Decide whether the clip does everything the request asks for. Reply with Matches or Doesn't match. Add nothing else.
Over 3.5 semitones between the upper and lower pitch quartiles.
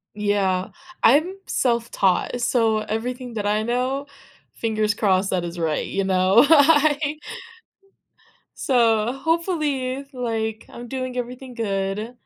Matches